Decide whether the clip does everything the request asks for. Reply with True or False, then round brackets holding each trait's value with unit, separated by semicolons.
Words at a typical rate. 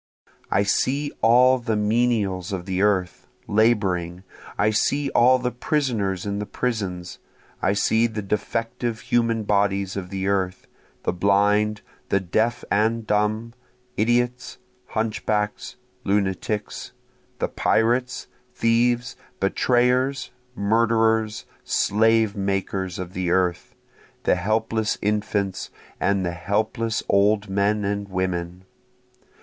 False (110 wpm)